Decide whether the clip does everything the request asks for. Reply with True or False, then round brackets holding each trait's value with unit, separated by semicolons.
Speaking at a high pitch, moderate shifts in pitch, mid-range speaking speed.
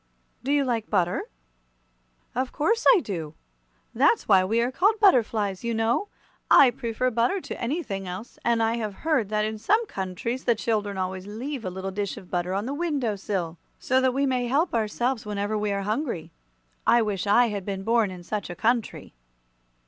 True (225 Hz; 4.4 semitones; 190 wpm)